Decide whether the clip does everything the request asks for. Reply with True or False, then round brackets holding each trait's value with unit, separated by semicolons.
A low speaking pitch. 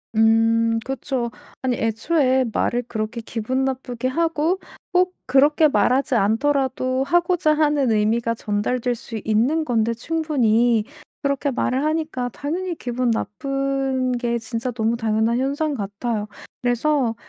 False (255 Hz)